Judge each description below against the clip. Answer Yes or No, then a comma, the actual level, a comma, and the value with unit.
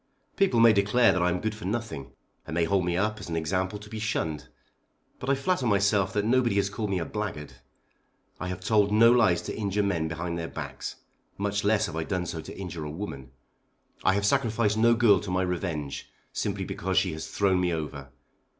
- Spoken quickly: Yes, fast, 215 wpm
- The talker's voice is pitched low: Yes, low, 100 Hz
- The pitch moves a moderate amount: Yes, average, 3.9 semitones